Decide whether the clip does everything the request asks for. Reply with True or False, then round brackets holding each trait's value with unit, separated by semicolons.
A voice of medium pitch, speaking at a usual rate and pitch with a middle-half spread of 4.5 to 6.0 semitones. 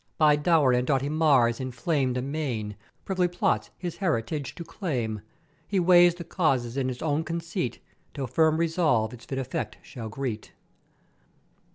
True (145 Hz; 150 wpm; 5.1 semitones)